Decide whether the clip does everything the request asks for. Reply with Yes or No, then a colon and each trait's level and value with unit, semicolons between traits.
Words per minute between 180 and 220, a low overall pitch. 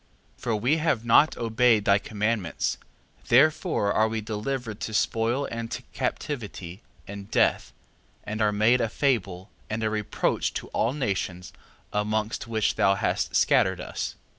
No: average, 150 wpm; low, 110 Hz